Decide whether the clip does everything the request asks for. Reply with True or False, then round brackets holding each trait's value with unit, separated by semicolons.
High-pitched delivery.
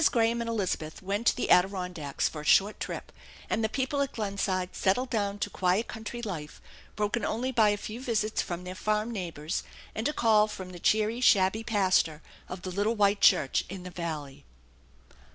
True (205 Hz)